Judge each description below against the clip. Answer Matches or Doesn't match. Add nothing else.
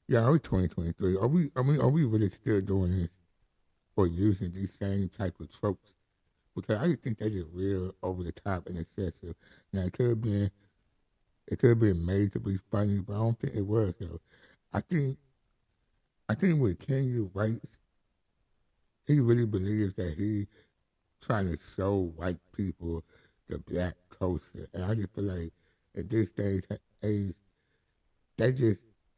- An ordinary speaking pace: Matches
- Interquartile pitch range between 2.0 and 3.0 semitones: Doesn't match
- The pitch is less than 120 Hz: Matches